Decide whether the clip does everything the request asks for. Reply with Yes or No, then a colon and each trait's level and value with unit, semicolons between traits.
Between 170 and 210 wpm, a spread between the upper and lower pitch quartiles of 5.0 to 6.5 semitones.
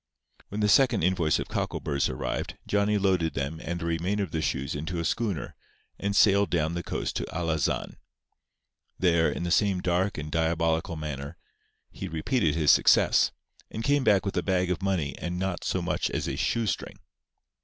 No: average, 180 wpm; average, 3.7 semitones